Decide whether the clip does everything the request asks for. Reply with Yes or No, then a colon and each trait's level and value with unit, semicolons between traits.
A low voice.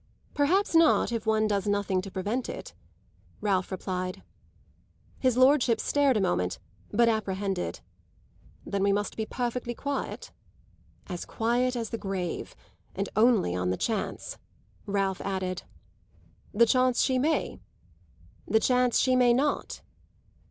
No: high, 220 Hz